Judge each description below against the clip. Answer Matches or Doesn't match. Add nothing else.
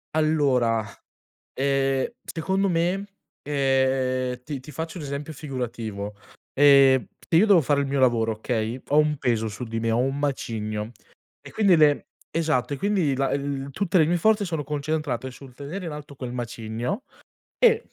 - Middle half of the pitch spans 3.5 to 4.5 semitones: Matches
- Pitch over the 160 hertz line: Doesn't match